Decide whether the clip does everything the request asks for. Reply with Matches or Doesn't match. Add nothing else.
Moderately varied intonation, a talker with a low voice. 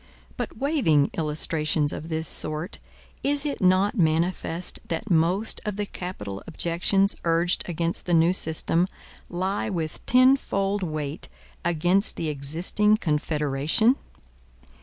Doesn't match